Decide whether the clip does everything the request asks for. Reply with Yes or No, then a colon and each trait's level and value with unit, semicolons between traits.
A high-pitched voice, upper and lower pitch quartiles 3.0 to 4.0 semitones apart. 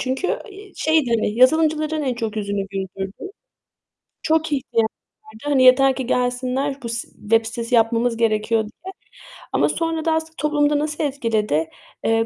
No: very high, 250 Hz; average, 4.9 semitones